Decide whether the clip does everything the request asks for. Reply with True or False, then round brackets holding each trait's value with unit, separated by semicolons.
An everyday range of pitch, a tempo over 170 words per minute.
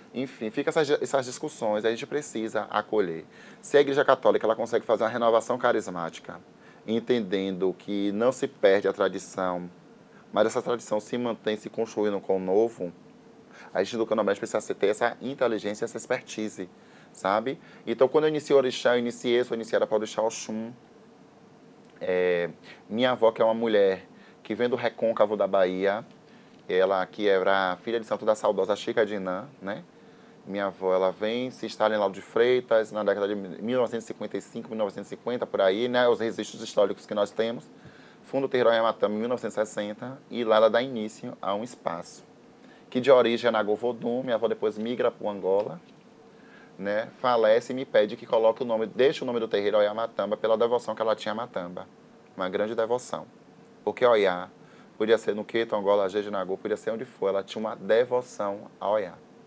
True (3.1 semitones; 180 wpm)